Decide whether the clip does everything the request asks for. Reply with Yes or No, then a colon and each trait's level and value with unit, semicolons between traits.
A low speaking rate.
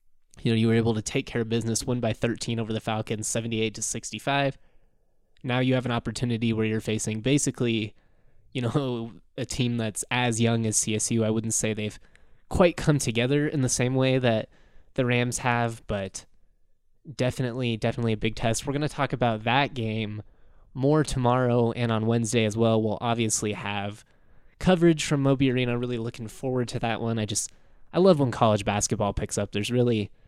No: average, 190 wpm